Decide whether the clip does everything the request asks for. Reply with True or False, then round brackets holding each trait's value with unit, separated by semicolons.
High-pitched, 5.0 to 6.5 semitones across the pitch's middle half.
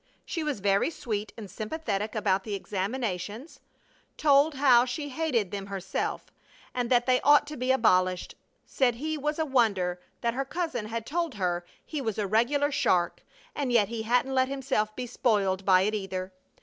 True (235 Hz; 5.4 semitones)